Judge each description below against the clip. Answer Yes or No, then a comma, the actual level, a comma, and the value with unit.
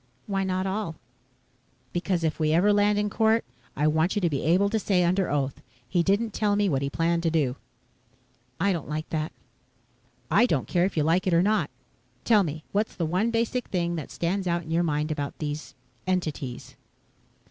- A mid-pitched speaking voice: Yes, medium, 175 Hz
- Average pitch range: Yes, average, 4.3 semitones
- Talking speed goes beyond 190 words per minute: Yes, average, 200 wpm